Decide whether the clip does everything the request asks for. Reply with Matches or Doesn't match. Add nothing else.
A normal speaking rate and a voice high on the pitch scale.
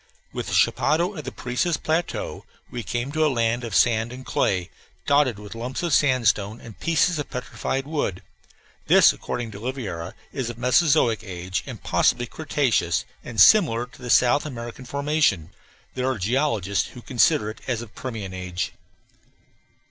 Doesn't match